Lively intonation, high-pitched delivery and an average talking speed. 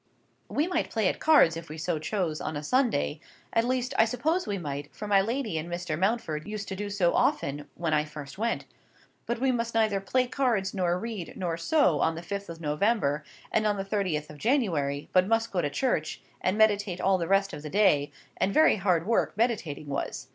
No: wide, 6.2 semitones; high, 195 Hz; fast, 210 wpm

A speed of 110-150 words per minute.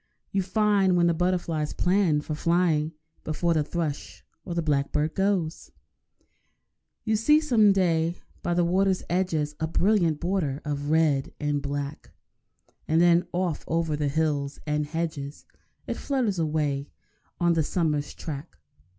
Yes: average, 140 wpm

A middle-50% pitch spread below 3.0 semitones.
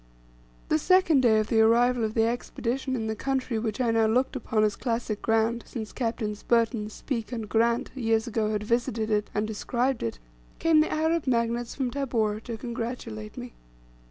Yes: narrow, 2.4 semitones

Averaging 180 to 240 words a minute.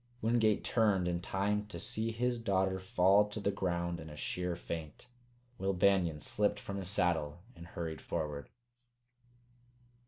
No: average, 150 wpm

